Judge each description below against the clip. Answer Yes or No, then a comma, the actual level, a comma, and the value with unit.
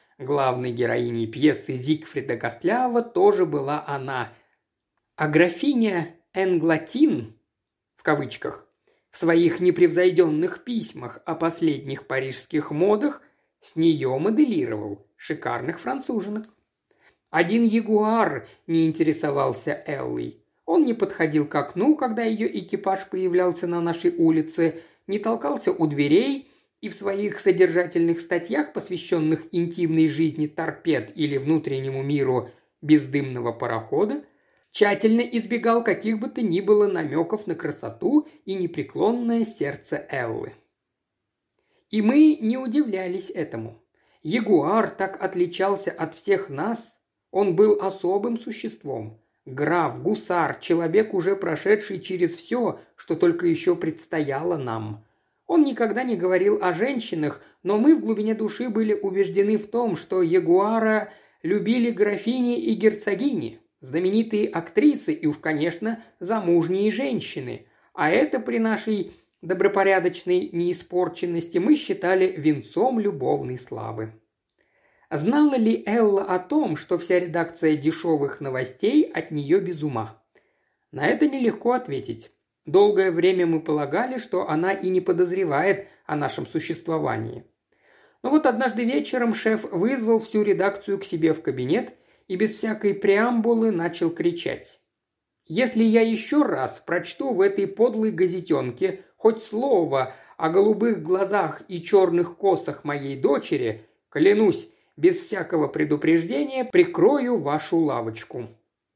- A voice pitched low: No, high, 190 Hz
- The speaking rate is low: No, average, 120 wpm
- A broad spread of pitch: Yes, wide, 6.0 semitones